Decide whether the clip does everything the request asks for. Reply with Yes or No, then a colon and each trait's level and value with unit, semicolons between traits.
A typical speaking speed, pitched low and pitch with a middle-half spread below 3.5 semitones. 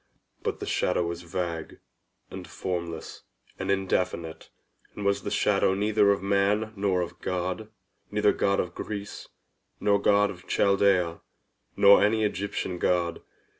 No: slow, 130 wpm; low, 100 Hz; narrow, 2.5 semitones